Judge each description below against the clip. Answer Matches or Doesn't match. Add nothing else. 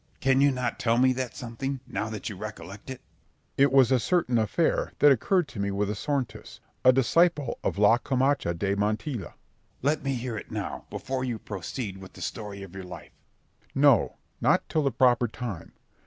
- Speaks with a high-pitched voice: Doesn't match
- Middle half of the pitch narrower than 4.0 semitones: Doesn't match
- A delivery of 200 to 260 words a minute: Matches